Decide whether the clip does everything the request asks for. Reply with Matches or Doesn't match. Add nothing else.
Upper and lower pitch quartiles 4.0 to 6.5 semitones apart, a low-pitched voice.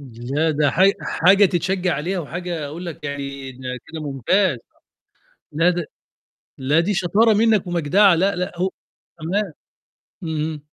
Doesn't match